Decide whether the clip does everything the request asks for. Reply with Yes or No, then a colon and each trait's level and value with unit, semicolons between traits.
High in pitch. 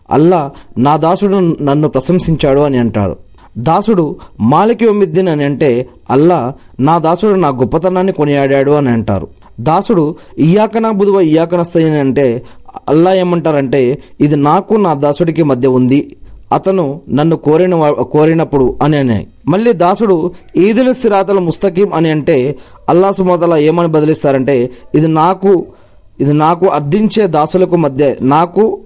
No: medium, 155 Hz